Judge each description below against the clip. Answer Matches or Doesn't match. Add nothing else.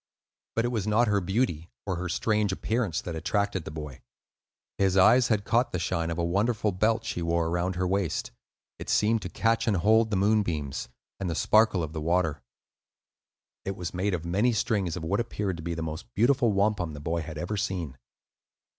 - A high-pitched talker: Doesn't match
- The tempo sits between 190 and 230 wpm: Matches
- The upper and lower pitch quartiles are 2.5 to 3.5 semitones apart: Doesn't match